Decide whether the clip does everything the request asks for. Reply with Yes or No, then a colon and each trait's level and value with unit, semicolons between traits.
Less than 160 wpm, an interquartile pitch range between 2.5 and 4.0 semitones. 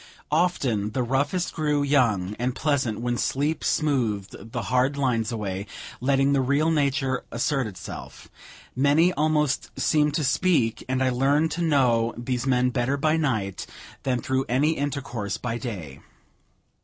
Yes: average, 145 wpm; average, 3.7 semitones